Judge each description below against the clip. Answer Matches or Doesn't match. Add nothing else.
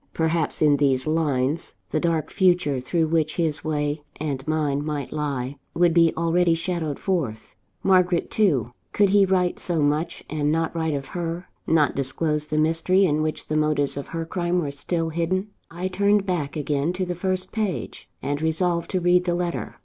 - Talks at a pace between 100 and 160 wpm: Doesn't match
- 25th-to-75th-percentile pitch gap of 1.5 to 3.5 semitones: Matches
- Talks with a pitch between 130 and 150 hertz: Doesn't match